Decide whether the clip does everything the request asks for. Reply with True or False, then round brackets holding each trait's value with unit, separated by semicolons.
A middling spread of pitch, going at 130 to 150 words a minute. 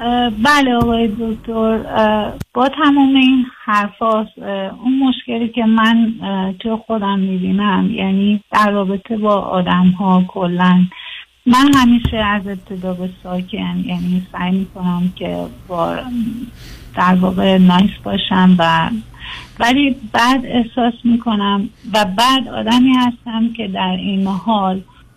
False (4.0 semitones; 115 wpm)